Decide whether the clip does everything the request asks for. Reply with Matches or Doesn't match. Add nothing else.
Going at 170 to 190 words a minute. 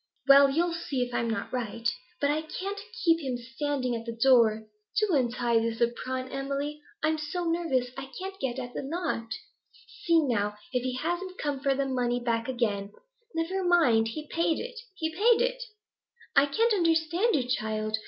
Matches